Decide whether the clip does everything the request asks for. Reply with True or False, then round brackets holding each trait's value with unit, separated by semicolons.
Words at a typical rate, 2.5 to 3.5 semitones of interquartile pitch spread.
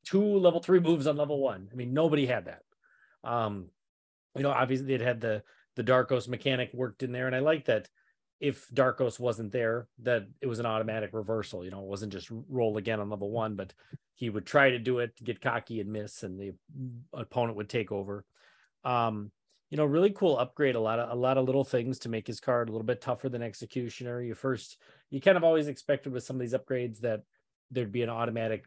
False (225 wpm; 3.0 semitones)